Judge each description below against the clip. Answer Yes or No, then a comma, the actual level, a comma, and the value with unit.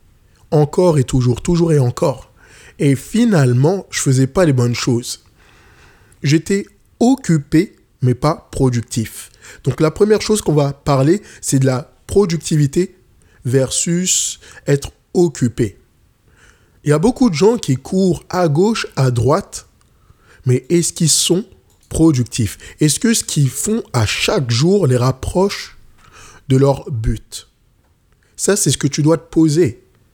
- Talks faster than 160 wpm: No, slow, 145 wpm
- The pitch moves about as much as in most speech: No, wide, 6.0 semitones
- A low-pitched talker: No, medium, 145 Hz